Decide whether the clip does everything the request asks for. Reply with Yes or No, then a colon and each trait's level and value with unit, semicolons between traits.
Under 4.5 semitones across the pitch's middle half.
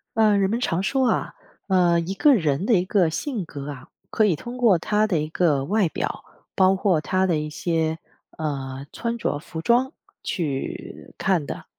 No: average, 5.3 semitones